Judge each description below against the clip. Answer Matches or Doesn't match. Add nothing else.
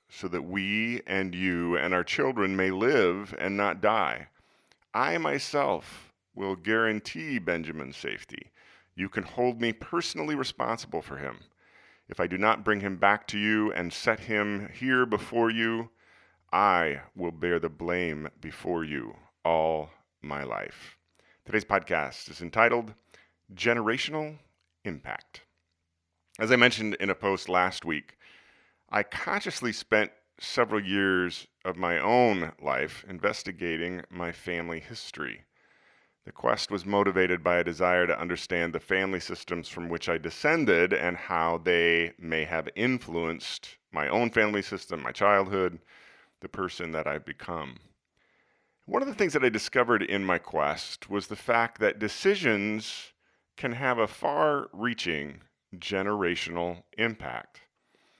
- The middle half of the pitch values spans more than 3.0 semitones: Matches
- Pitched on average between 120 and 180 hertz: Doesn't match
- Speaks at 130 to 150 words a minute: Matches